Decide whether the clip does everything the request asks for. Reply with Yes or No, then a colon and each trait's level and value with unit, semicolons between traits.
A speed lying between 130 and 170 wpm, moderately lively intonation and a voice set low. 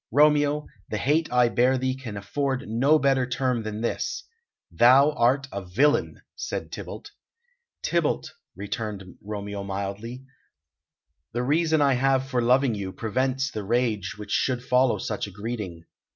Yes: average, 145 wpm; average, 4.4 semitones; low, 125 Hz